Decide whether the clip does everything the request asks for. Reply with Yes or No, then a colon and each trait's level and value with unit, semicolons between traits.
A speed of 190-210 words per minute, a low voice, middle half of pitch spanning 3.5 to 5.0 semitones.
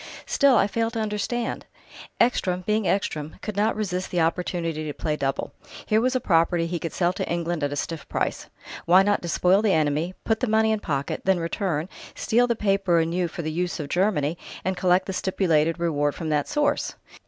No: average, 200 wpm; medium, 180 Hz; average, 4.2 semitones